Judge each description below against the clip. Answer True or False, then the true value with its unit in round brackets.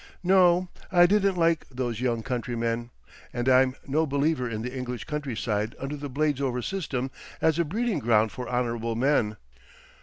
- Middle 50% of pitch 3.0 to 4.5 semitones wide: False (4.9 semitones)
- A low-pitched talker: True (130 Hz)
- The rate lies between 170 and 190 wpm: False (155 wpm)